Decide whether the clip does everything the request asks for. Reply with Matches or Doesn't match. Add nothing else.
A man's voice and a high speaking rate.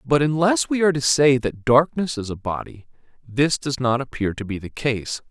Matches